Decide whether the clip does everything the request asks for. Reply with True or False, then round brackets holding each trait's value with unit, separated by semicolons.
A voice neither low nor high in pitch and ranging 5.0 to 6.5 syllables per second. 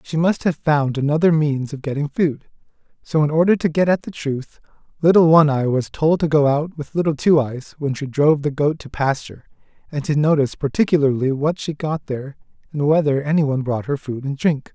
True (150 Hz; 5.5 syllables/s)